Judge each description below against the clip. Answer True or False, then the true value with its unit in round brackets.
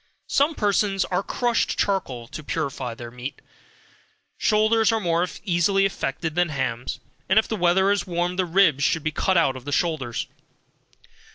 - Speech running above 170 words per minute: False (165 wpm)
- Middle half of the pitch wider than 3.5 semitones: True (5.5 semitones)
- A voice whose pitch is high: False (175 Hz)